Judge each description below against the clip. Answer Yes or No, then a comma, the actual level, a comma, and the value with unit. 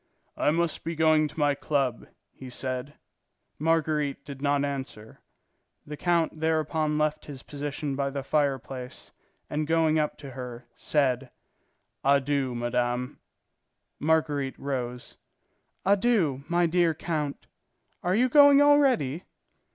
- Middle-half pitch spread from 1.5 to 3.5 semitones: Yes, average, 3.0 semitones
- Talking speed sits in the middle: No, slow, 120 wpm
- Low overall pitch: No, medium, 145 Hz